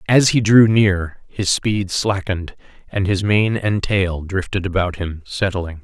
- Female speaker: No, male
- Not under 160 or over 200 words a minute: Yes, average, 165 wpm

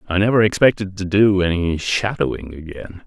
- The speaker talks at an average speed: Yes, average, 155 wpm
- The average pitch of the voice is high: No, very low, 95 Hz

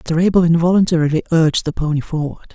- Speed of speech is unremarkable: Yes, average, 165 wpm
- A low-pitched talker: No, medium, 160 Hz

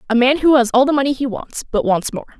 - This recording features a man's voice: No, female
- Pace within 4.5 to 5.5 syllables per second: No, 6.4 syllables/s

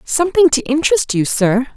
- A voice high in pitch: Yes, very high, 285 Hz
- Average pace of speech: Yes, average, 170 wpm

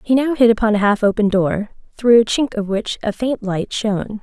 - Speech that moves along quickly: Yes, fast, 240 wpm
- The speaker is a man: No, female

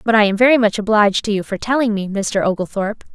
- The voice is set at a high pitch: Yes, high, 210 Hz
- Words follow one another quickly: Yes, fast, 250 wpm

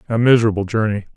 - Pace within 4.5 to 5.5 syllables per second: No, 7.8 syllables/s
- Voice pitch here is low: Yes, low, 110 Hz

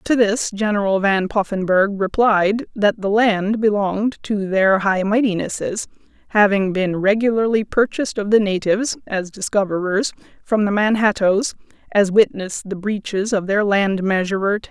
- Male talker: No, female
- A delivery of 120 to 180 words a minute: Yes, average, 145 wpm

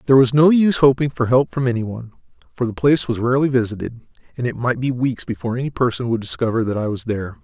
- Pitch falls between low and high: No, low, 125 Hz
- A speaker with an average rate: No, fast, 240 wpm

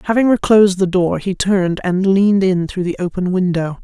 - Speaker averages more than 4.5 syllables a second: Yes, 5.5 syllables/s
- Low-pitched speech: No, medium, 185 Hz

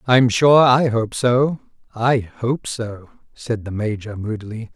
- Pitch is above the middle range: No, low, 120 Hz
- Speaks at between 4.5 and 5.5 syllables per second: No, 3.7 syllables/s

